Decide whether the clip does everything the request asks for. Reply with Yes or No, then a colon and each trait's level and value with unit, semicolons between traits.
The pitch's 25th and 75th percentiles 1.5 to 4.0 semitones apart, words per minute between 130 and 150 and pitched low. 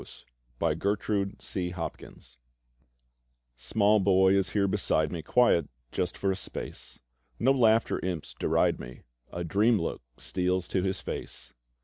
Yes: average, 3.0 semitones; slow, 135 wpm; very low, 95 Hz